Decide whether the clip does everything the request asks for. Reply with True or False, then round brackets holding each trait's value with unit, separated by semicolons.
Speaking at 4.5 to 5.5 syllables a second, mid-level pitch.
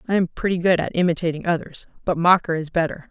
False (6.2 syllables/s; 170 Hz)